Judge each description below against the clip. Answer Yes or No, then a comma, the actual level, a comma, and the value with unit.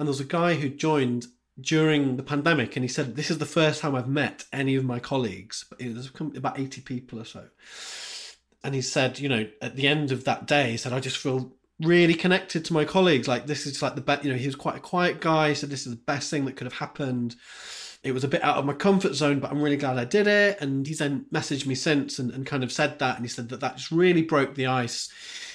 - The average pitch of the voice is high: No, medium, 140 Hz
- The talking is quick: Yes, fast, 270 wpm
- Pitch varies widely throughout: No, average, 3.1 semitones